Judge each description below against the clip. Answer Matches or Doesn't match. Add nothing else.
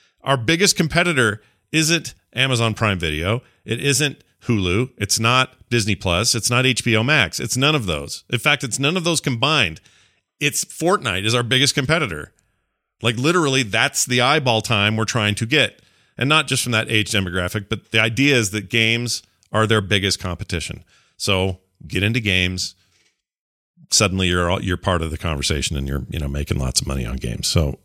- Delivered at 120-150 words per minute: Doesn't match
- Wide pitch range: Matches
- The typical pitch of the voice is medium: Doesn't match